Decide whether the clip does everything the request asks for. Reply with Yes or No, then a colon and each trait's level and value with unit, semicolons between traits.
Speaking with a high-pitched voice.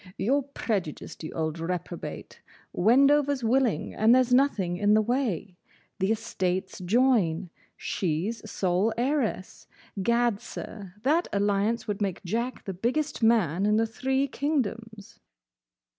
Yes: high, 220 Hz